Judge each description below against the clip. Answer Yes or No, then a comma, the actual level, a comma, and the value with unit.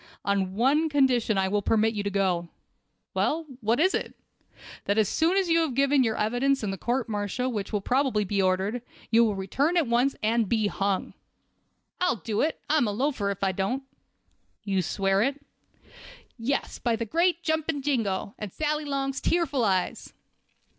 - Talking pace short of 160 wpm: No, average, 180 wpm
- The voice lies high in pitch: Yes, high, 230 Hz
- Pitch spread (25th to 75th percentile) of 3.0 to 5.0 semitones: No, wide, 5.6 semitones